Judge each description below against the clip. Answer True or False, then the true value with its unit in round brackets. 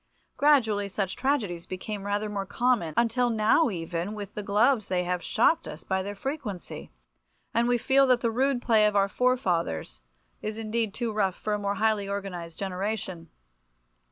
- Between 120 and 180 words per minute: True (170 wpm)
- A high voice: True (210 Hz)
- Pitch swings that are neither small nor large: True (3.7 semitones)